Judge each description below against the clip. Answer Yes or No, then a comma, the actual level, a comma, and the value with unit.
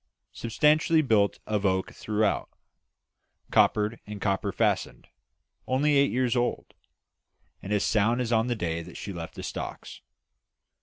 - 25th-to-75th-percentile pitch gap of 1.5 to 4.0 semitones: Yes, average, 3.7 semitones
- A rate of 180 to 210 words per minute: No, average, 140 wpm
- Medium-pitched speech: No, low, 110 Hz